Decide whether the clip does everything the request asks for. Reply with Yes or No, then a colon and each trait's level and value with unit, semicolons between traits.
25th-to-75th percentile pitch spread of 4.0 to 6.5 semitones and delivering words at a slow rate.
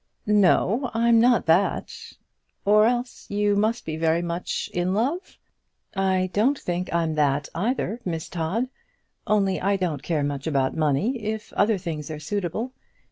No: average, 5.1 semitones; average, 155 wpm